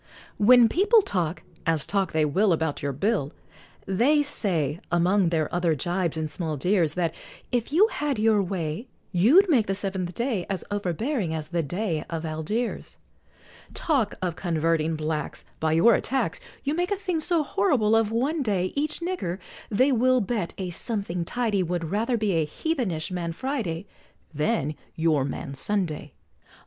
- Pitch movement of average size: No, wide, 6.5 semitones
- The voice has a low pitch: No, high, 190 Hz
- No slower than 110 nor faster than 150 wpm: No, average, 160 wpm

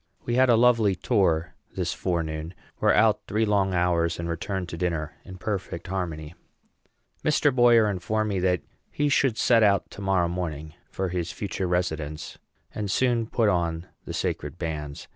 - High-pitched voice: No, very low, 90 Hz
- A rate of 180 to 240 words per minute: No, average, 165 wpm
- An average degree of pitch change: Yes, average, 4.4 semitones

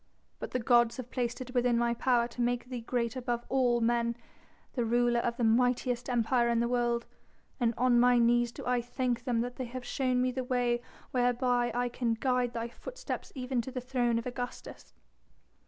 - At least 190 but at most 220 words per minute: Yes, average, 200 wpm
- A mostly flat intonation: Yes, narrow, 0.9 semitones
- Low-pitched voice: No, high, 245 Hz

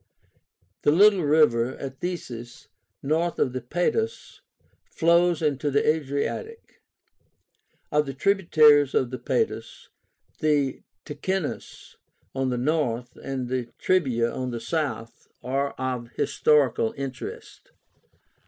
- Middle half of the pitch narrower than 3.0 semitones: No, average, 4.1 semitones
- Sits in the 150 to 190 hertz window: No, medium, 140 Hz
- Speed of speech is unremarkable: No, slow, 105 wpm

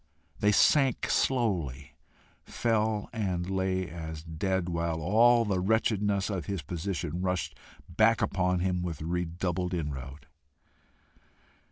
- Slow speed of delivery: Yes, slow, 115 wpm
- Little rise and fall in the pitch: No, average, 3.7 semitones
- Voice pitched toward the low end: Yes, very low, 90 Hz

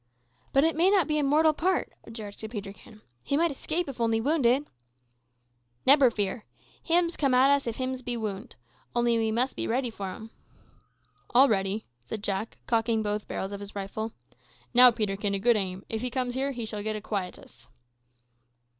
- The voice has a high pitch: Yes, high, 230 Hz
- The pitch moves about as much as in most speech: Yes, average, 4.5 semitones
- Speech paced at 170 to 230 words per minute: Yes, average, 180 wpm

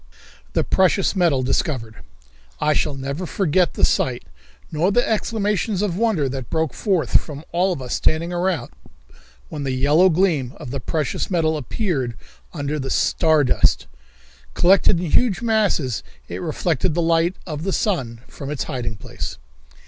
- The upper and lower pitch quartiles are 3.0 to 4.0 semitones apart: No, average, 5.3 semitones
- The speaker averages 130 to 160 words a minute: Yes, average, 155 wpm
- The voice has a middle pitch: Yes, medium, 160 Hz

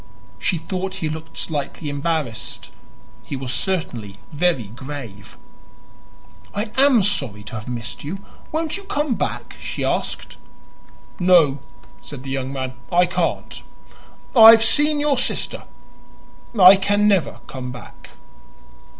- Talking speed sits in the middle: No, slow, 130 wpm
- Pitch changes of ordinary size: No, wide, 7.6 semitones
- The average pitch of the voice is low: No, medium, 165 Hz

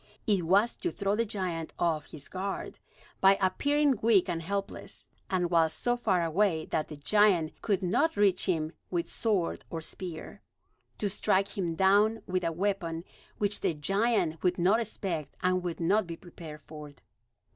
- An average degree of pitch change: Yes, average, 3.8 semitones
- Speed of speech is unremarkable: Yes, average, 165 wpm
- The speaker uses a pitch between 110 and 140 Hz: No, medium, 185 Hz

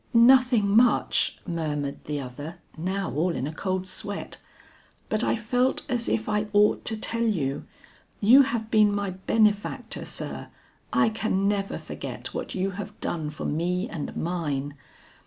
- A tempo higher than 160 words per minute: No, average, 155 wpm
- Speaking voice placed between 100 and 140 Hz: No, high, 200 Hz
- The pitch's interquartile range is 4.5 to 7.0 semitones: Yes, average, 5.0 semitones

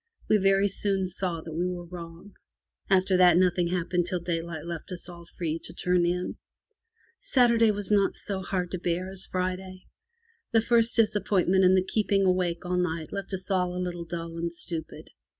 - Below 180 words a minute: No, average, 190 wpm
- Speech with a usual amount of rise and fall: No, narrow, 2.0 semitones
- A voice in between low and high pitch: Yes, medium, 180 Hz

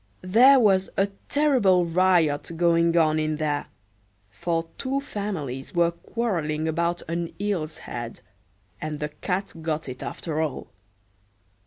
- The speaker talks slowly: Yes, slow, 130 wpm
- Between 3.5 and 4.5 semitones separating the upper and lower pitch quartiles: Yes, average, 3.8 semitones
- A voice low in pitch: No, medium, 170 Hz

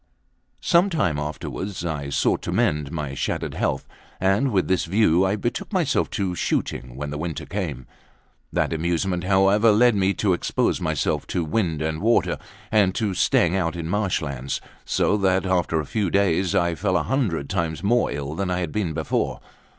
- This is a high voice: No, very low, 90 Hz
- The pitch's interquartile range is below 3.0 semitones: No, average, 4.2 semitones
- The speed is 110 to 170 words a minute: No, average, 185 wpm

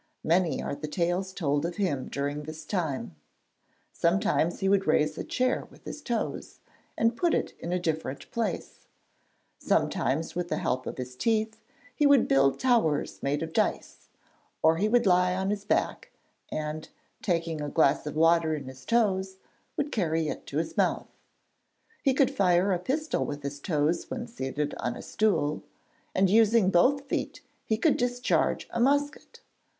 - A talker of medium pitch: Yes, medium, 175 Hz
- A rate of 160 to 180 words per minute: Yes, average, 170 wpm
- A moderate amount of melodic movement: No, wide, 6.5 semitones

